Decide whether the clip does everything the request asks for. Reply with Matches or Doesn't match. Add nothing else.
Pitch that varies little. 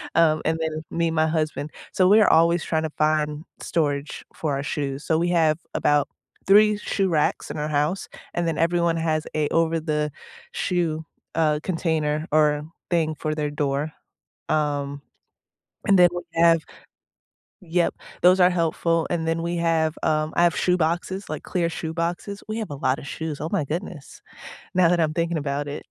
Matches